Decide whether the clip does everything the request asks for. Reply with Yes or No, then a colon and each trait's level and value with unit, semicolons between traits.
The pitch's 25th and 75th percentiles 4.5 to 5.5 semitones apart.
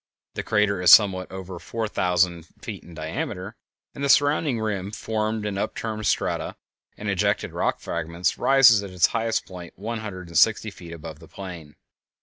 No: average, 3.6 semitones